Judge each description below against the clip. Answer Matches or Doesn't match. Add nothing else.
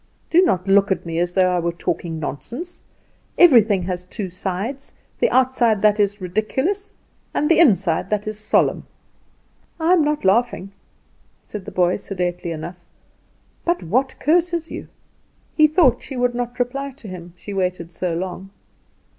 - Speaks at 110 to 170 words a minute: Matches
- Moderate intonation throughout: Doesn't match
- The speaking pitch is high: Matches